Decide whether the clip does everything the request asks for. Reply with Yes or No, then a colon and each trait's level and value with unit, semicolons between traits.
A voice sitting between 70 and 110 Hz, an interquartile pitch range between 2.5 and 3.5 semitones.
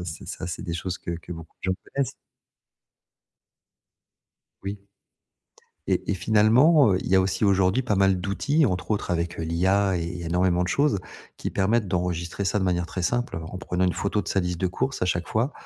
Yes: very low, 95 Hz; average, 2.9 semitones